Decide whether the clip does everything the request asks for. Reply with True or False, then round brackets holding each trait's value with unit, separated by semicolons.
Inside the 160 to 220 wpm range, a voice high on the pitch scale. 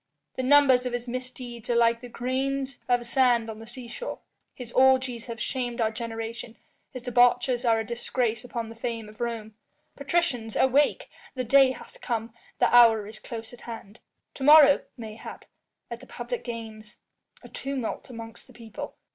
True (170 wpm; 240 Hz)